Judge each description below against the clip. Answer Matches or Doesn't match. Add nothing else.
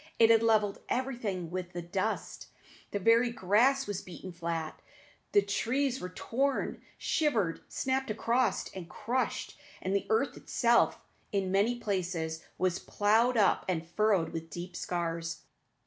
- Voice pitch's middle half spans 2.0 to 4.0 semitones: Doesn't match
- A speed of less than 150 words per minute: Matches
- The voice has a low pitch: Doesn't match